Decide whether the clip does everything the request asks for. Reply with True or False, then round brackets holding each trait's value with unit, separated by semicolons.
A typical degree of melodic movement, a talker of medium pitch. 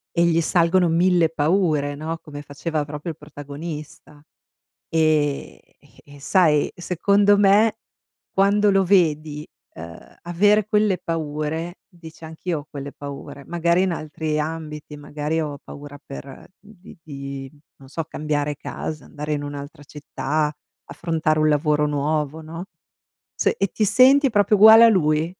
True (3.1 semitones; 155 Hz)